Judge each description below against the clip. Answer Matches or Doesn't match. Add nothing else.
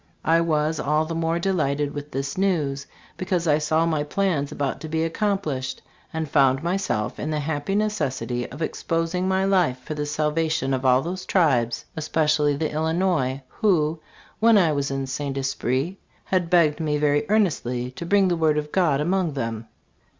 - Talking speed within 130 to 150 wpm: Doesn't match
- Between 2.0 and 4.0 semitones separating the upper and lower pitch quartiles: Matches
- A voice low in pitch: Doesn't match